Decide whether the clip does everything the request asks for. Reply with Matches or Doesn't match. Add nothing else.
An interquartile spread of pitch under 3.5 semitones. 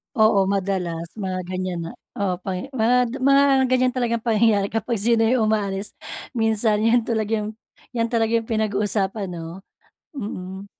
Matches